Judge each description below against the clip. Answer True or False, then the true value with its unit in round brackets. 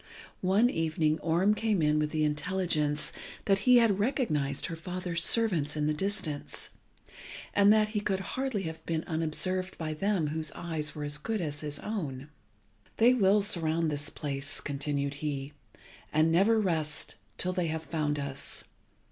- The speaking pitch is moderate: True (160 Hz)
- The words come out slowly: False (160 wpm)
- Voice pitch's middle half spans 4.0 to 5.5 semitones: True (4.6 semitones)